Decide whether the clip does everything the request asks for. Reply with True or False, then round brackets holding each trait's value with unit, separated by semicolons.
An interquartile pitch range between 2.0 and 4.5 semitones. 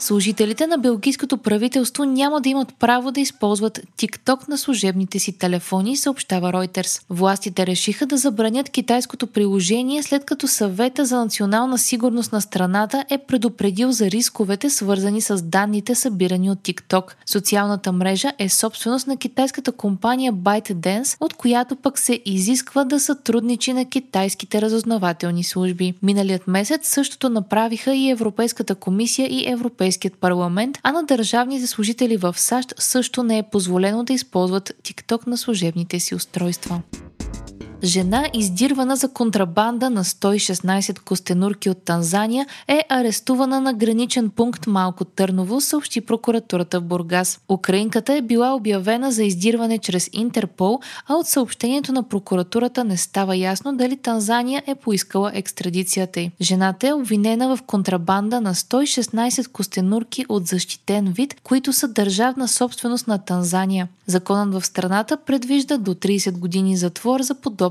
False (5.0 semitones)